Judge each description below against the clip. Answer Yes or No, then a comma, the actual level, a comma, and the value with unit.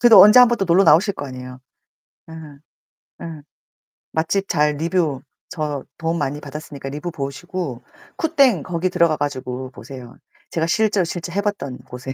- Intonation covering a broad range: No, average, 5.0 semitones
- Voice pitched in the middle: Yes, medium, 160 Hz